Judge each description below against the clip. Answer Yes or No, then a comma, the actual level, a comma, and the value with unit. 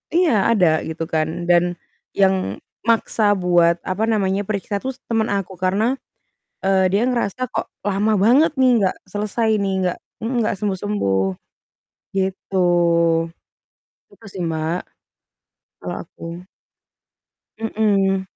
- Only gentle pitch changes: No, average, 3.1 semitones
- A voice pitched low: No, high, 195 Hz